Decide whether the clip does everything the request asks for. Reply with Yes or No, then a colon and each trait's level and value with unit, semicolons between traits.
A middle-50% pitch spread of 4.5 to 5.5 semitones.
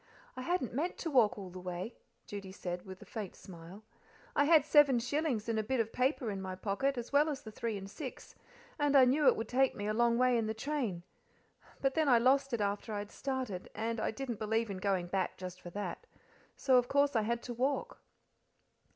Yes: average, 5.0 semitones